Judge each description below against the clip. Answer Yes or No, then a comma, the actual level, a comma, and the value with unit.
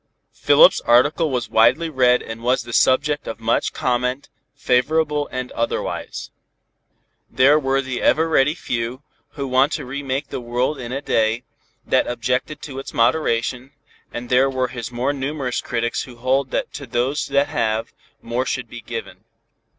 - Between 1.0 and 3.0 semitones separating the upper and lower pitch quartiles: Yes, average, 2.7 semitones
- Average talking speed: Yes, average, 165 wpm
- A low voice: Yes, low, 130 Hz